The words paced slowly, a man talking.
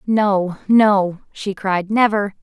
No: slow, 125 wpm; female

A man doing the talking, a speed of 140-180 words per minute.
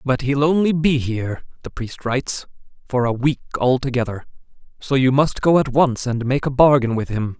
No: male; average, 195 wpm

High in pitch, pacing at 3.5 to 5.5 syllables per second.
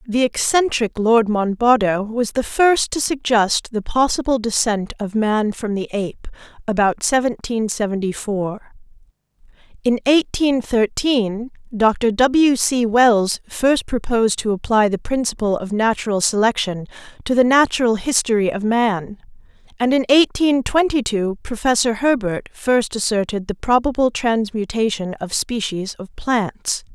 Yes: high, 230 Hz; 4.2 syllables/s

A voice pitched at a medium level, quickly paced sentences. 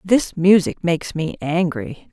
No: medium, 175 Hz; average, 140 wpm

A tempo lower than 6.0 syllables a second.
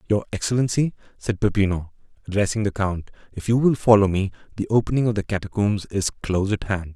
No: 6.2 syllables/s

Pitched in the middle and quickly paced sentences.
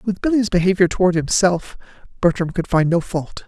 No: medium, 180 Hz; average, 170 wpm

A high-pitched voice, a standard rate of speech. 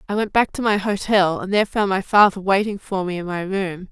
No: high, 195 Hz; fast, 260 wpm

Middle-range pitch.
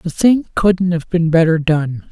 Yes: medium, 170 Hz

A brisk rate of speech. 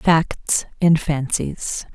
No: slow, 95 wpm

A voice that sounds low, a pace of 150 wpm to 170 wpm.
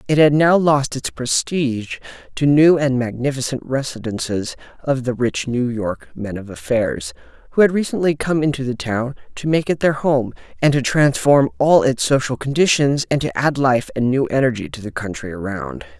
No: low, 130 Hz; average, 185 wpm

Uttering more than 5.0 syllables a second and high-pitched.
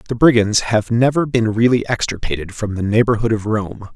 No: 5.4 syllables/s; low, 110 Hz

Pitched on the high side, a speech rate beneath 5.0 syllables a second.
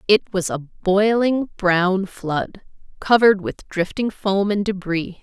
Yes: high, 195 Hz; 3.6 syllables/s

